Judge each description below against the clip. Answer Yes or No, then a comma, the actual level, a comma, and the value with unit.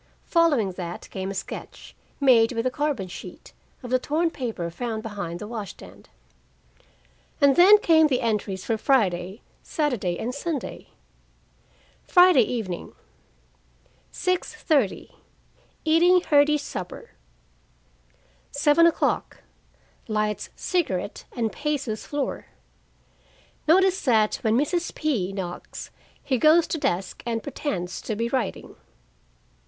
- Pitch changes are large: Yes, wide, 6.5 semitones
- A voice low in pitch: No, high, 245 Hz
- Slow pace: Yes, slow, 115 wpm